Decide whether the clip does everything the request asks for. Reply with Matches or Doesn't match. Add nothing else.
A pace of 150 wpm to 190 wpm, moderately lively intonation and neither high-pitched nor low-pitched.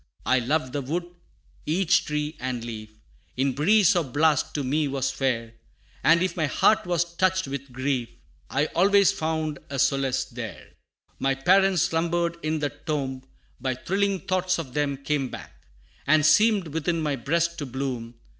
Matches